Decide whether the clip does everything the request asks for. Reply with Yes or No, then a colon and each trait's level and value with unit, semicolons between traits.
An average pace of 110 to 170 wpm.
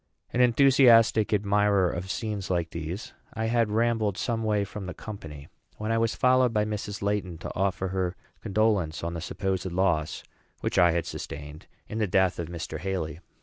No: average, 180 wpm